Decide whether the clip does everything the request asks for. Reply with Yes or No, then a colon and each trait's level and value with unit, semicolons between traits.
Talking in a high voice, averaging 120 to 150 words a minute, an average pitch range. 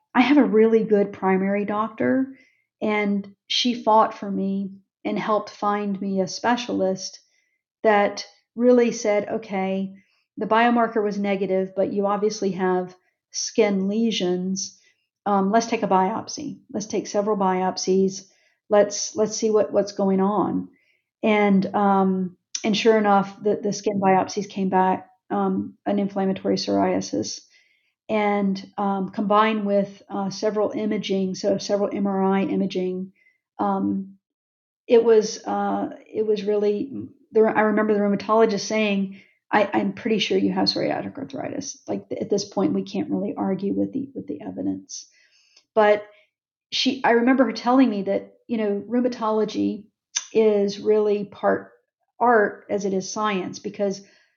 No: high, 205 Hz; average, 140 wpm; narrow, 2.2 semitones